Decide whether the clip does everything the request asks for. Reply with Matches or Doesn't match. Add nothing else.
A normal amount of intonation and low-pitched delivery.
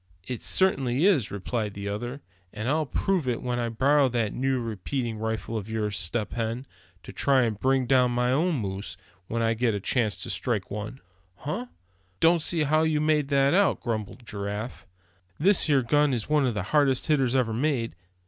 Matches